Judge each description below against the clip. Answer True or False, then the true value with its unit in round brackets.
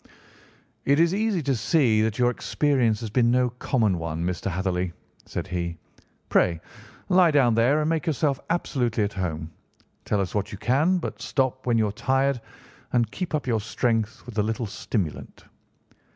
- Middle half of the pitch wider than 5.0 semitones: True (5.4 semitones)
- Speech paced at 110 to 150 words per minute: False (175 wpm)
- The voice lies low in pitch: True (120 Hz)